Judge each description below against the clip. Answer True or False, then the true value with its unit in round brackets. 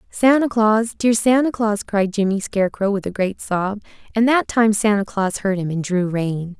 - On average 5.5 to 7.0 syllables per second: False (4.7 syllables/s)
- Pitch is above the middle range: True (210 Hz)